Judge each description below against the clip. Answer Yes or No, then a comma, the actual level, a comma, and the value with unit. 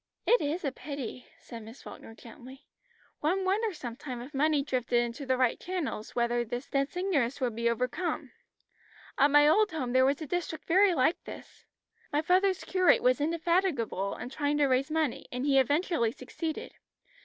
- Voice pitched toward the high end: Yes, very high, 280 Hz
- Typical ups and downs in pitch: Yes, average, 5.0 semitones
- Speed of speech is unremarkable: Yes, average, 175 wpm